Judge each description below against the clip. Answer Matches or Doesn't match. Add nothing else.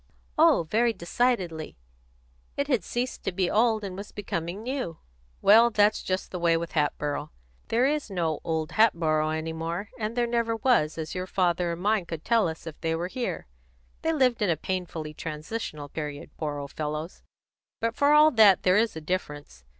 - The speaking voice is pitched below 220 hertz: Matches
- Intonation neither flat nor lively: Doesn't match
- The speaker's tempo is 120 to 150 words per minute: Doesn't match